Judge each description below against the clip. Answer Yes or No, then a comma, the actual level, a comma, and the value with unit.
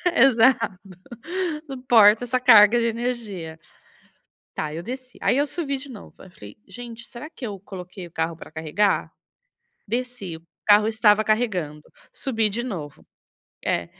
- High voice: Yes, high, 220 Hz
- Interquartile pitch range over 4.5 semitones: Yes, average, 5.2 semitones